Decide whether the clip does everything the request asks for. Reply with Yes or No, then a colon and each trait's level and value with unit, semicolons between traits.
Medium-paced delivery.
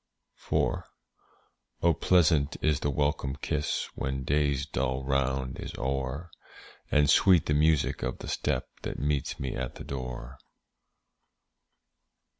No: slow, 125 wpm